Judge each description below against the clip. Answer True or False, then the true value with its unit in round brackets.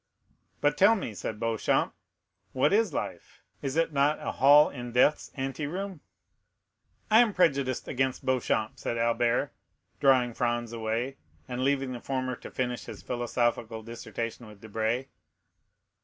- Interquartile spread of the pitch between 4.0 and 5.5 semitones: False (3.1 semitones)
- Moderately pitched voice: False (130 Hz)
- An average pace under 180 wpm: True (140 wpm)